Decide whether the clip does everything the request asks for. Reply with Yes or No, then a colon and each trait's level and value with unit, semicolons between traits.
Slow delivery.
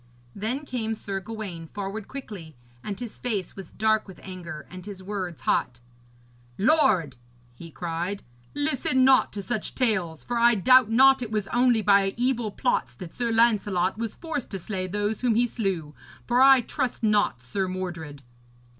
No: average, 165 wpm